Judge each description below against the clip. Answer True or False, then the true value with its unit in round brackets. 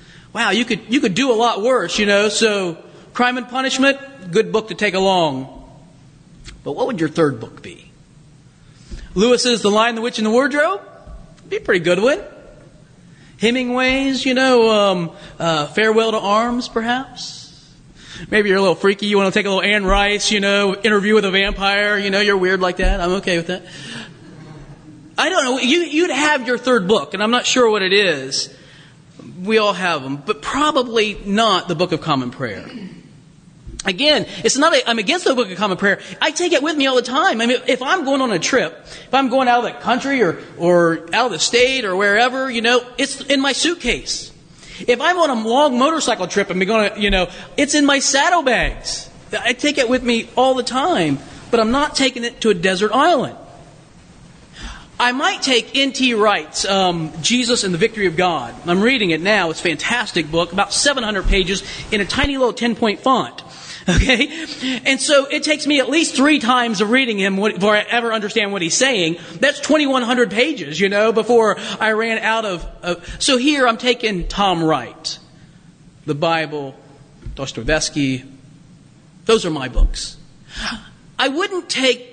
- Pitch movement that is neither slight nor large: False (6.7 semitones)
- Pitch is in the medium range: False (215 Hz)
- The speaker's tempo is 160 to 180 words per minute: False (195 wpm)